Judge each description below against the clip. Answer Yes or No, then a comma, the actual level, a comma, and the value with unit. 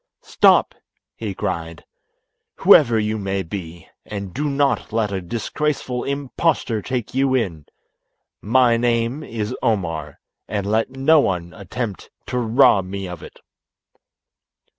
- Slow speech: Yes, slow, 125 wpm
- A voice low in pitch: Yes, low, 110 Hz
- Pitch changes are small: No, average, 4.8 semitones